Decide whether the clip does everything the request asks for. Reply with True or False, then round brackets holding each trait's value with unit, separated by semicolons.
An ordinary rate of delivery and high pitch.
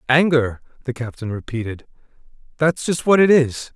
False (145 wpm; 135 Hz)